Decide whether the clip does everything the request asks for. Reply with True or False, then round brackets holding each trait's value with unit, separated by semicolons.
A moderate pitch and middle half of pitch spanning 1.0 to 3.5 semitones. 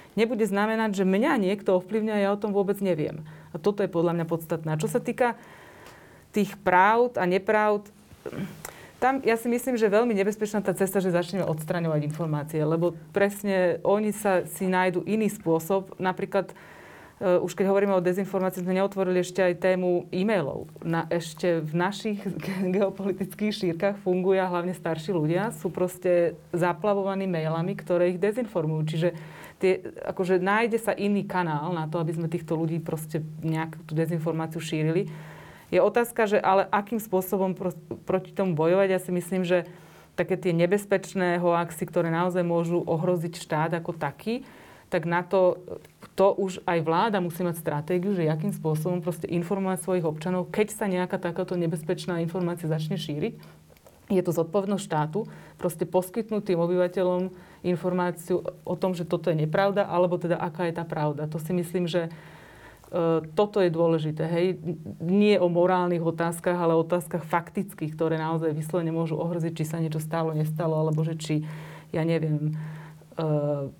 True (180 Hz; 2.8 semitones)